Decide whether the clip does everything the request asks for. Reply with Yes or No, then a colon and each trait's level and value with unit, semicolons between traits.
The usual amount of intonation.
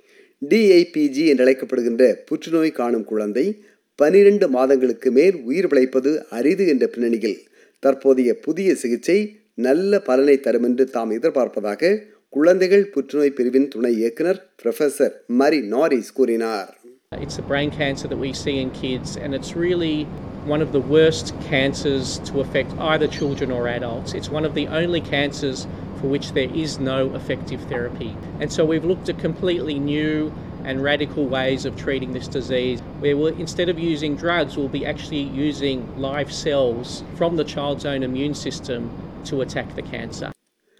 Yes: average, 3.3 semitones